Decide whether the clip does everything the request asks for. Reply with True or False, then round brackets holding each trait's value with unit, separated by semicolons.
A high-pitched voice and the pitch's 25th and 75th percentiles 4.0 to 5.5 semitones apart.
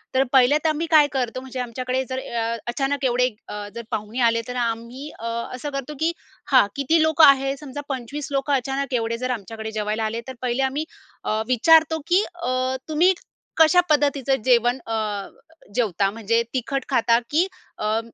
False (260 Hz; 3.5 semitones)